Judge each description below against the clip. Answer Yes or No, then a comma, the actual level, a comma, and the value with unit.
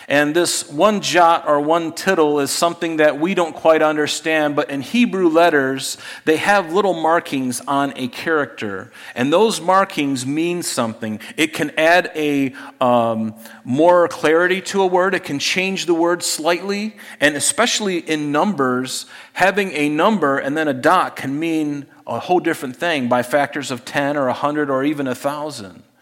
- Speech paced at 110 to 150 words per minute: No, average, 170 wpm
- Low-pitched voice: No, medium, 155 Hz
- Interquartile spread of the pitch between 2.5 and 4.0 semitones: Yes, average, 3.7 semitones